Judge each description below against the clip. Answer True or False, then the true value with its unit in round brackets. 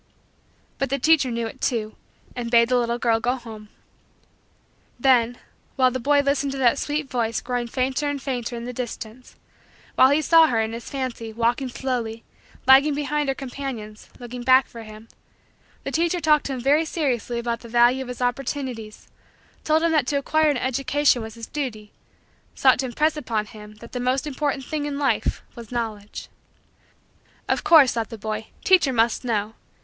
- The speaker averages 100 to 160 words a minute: False (185 wpm)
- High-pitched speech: True (250 Hz)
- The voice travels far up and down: False (3.2 semitones)